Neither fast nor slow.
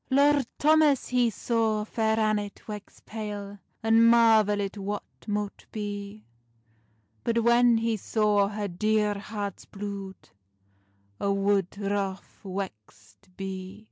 No: slow, 110 wpm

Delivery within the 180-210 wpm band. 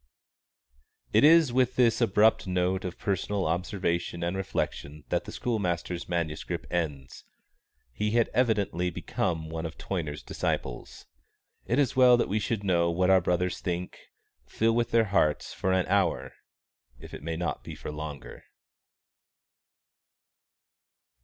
No: average, 140 wpm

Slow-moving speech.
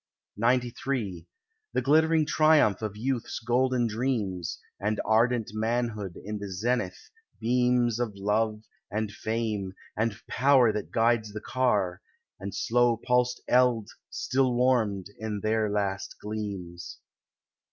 Yes: slow, 120 wpm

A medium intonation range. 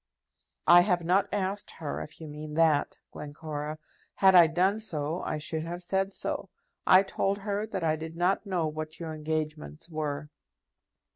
Yes: average, 3.5 semitones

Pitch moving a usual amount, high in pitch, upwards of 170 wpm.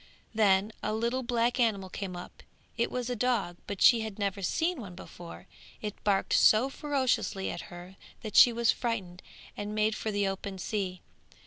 Yes: average, 3.5 semitones; high, 215 Hz; average, 180 wpm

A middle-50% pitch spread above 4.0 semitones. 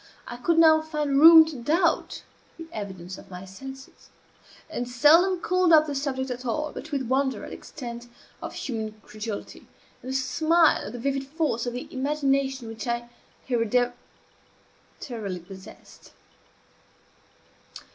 Yes: average, 4.4 semitones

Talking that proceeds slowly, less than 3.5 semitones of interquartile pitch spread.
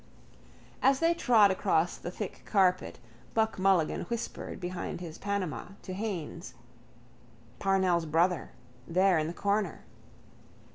Yes: slow, 115 wpm; average, 2.9 semitones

